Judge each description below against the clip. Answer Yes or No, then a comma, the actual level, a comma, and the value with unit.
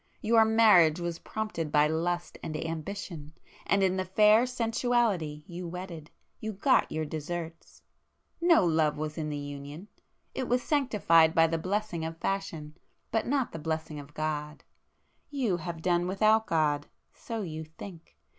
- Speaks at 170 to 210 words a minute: No, average, 150 wpm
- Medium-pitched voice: Yes, medium, 170 Hz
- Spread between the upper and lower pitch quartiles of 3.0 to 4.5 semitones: No, average, 5.3 semitones